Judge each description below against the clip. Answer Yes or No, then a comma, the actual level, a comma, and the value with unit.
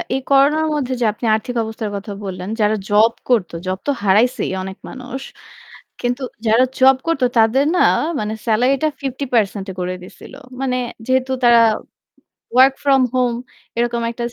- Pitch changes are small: No, average, 3.6 semitones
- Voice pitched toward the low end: No, high, 240 Hz